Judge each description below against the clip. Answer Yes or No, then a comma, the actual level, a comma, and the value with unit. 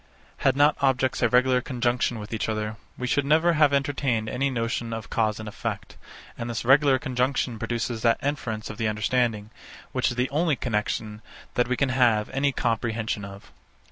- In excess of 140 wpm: Yes, average, 180 wpm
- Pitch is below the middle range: Yes, low, 120 Hz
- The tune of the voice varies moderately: Yes, average, 3.3 semitones